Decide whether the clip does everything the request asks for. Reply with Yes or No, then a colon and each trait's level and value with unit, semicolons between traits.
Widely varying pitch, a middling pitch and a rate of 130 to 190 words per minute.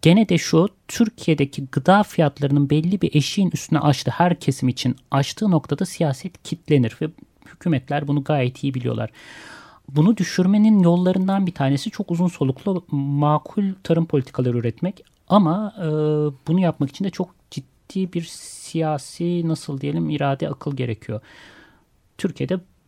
No: average, 4.3 semitones; medium, 155 Hz; average, 135 wpm